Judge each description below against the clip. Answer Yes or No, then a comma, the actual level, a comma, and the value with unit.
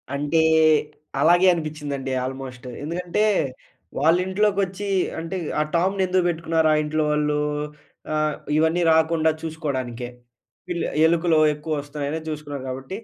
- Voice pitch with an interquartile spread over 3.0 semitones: No, average, 2.7 semitones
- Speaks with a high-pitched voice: No, medium, 160 Hz